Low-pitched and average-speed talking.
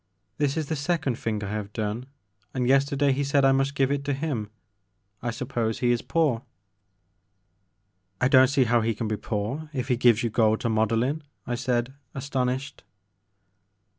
Yes: low, 125 Hz; average, 180 wpm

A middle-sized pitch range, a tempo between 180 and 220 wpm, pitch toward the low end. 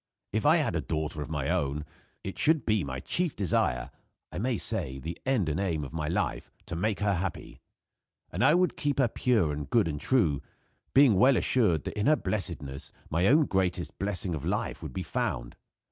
No: wide, 7.6 semitones; average, 200 wpm; very low, 95 Hz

